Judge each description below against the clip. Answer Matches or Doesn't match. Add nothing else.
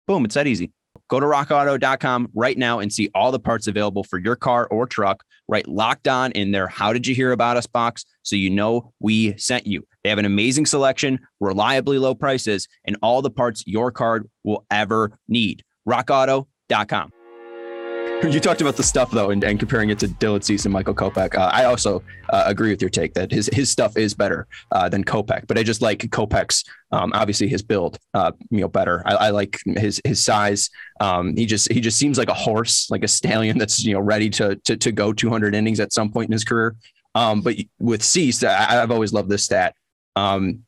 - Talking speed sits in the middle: Doesn't match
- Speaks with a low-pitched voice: Matches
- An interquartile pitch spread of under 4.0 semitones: Matches